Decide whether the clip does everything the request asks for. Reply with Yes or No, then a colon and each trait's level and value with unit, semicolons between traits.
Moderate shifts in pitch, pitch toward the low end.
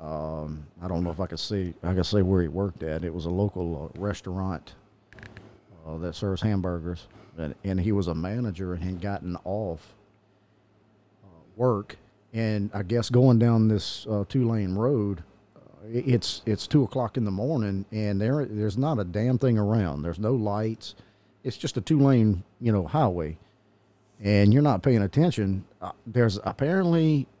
Yes: average, 3.6 semitones; low, 105 Hz